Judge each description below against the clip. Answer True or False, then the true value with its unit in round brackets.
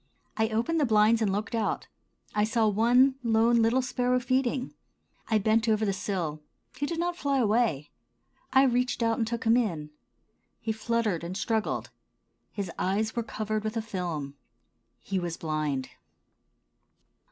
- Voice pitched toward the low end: False (220 Hz)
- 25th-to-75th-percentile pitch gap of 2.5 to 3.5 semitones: True (3.2 semitones)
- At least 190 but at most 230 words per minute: False (155 wpm)